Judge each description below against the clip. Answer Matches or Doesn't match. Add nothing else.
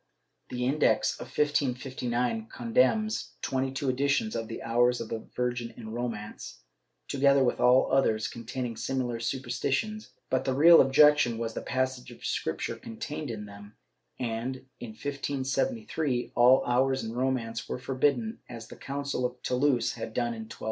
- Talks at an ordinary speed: Matches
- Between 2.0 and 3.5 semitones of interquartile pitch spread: Matches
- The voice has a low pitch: Matches